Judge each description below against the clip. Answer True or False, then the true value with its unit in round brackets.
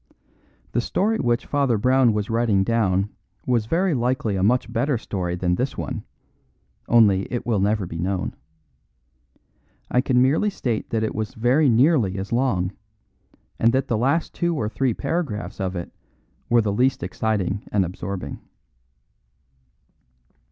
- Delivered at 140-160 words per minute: True (150 wpm)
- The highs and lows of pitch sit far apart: False (4.6 semitones)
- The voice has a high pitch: False (115 Hz)